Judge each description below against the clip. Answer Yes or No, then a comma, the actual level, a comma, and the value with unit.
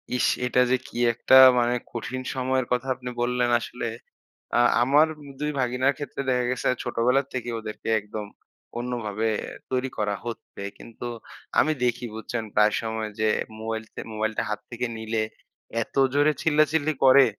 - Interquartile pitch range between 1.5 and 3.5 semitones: Yes, average, 2.8 semitones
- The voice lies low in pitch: Yes, low, 125 Hz